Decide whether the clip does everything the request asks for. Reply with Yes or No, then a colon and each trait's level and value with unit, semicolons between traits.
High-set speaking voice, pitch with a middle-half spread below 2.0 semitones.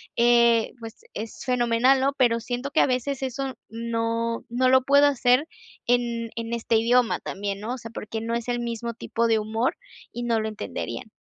Yes: high, 235 Hz; narrow, 1.6 semitones